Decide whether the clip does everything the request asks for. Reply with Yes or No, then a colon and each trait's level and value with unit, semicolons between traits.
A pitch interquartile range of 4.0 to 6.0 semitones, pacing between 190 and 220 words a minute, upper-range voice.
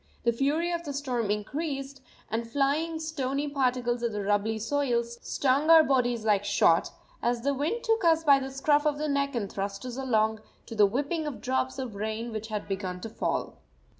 Yes: average, 4.6 semitones; average, 195 wpm; very high, 255 Hz